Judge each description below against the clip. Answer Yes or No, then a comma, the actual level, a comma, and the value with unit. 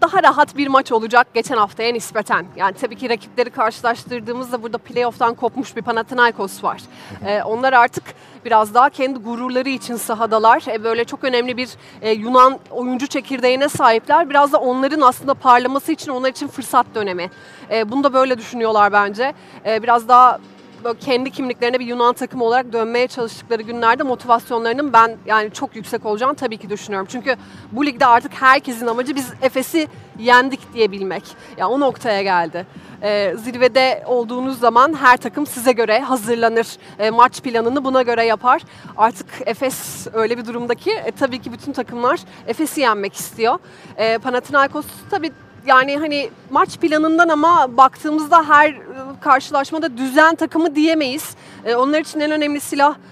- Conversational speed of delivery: No, fast, 150 wpm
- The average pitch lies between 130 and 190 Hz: No, very high, 250 Hz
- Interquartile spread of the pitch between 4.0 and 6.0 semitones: No, average, 3.0 semitones